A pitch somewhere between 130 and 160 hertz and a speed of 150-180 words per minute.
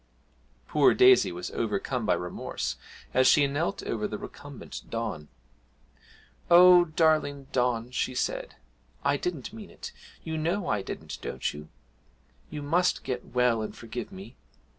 No: medium, 140 Hz; average, 140 wpm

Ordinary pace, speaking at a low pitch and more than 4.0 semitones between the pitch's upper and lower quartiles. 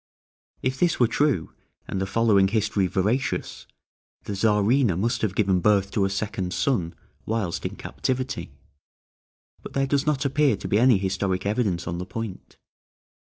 Yes: average, 155 wpm; low, 105 Hz; average, 4.7 semitones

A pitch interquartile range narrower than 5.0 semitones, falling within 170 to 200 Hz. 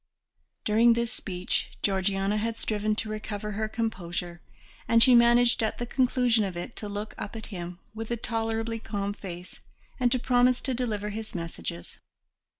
No: average, 2.9 semitones; high, 215 Hz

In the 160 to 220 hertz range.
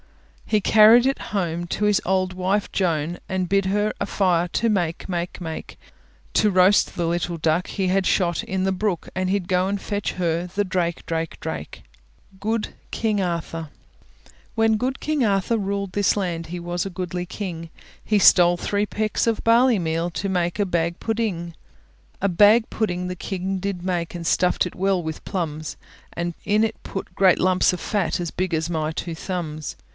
Yes: medium, 185 Hz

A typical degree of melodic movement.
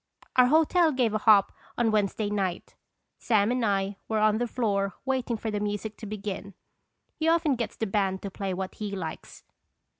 Yes: average, 3.3 semitones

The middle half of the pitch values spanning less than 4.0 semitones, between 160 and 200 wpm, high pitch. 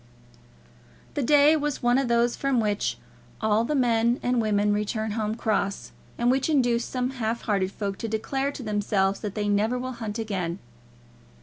Yes: average, 3.2 semitones; average, 175 wpm; high, 225 Hz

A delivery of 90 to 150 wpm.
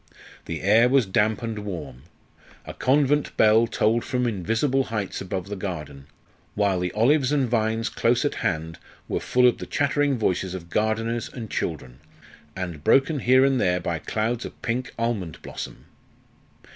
No: average, 160 wpm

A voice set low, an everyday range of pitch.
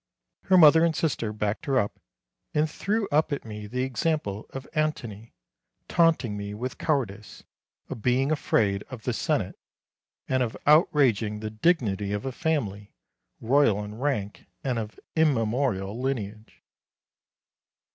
No: low, 125 Hz; wide, 5.7 semitones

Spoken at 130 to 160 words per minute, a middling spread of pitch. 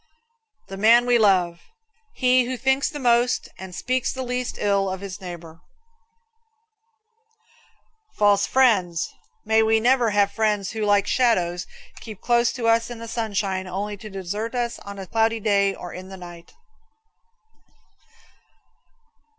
Yes: average, 140 wpm; average, 3.7 semitones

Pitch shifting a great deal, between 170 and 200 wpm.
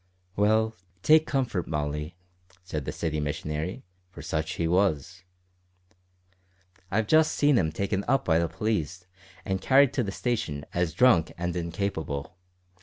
No: wide, 5.8 semitones; average, 140 wpm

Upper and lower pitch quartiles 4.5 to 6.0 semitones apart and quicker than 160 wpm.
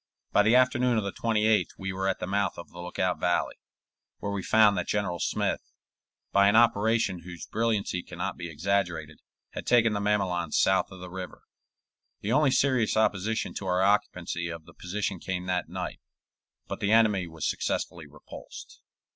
No: average, 3.4 semitones; average, 180 wpm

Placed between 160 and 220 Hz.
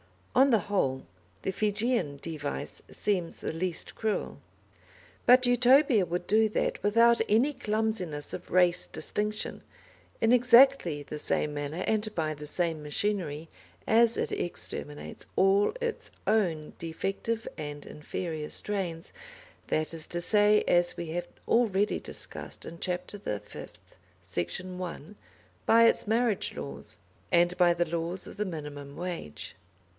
Yes: medium, 185 Hz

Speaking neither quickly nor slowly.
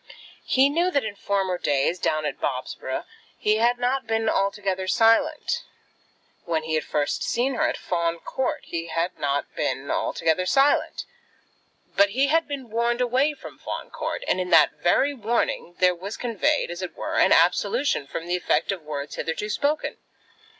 Yes: average, 170 wpm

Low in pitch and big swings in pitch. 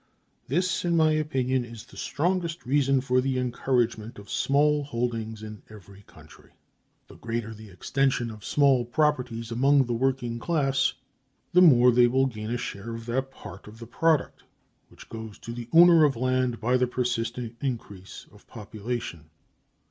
No: low, 125 Hz; average, 3.1 semitones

